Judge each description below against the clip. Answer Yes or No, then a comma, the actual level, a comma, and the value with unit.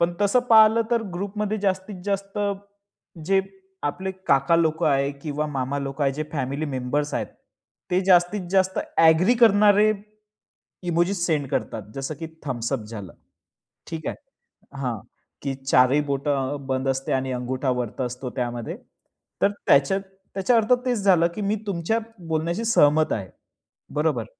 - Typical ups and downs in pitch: No, wide, 6.4 semitones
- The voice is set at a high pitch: No, medium, 155 Hz